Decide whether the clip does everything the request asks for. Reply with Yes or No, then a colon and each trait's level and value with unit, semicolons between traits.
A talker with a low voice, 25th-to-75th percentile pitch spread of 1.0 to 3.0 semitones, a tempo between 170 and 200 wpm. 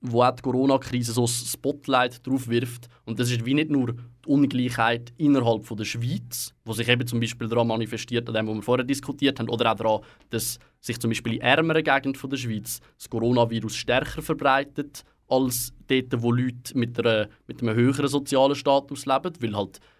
Yes: low, 120 Hz; average, 2.7 semitones; fast, 190 wpm